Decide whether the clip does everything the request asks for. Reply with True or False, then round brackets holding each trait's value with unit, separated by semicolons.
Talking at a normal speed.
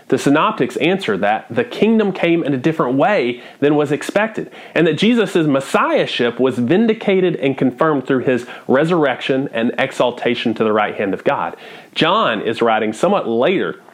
True (165 wpm)